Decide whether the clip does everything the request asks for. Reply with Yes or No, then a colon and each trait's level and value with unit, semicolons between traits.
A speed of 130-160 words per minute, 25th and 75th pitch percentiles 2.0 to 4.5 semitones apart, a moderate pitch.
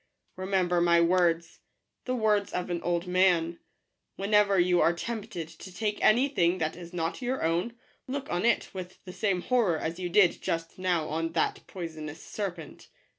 No: average, 180 wpm; average, 3.2 semitones; medium, 180 Hz